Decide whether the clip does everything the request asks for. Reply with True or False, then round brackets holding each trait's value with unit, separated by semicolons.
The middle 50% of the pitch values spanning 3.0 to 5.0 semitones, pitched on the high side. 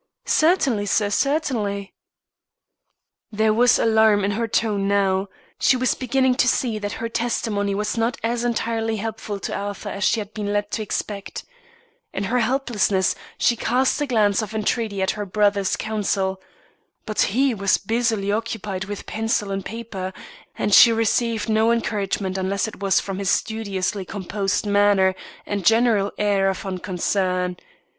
False (2.5 semitones; 210 Hz)